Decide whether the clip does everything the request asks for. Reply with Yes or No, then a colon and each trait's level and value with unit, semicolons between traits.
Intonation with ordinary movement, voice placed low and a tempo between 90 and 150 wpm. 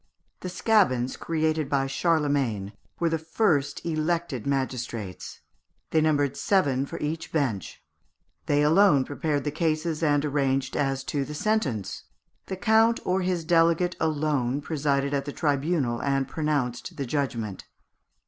No: average, 3.3 semitones; medium, 145 Hz; slow, 135 wpm